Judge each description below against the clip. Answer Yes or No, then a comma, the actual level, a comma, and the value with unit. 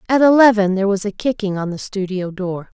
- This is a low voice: No, high, 205 Hz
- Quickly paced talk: Yes, fast, 215 wpm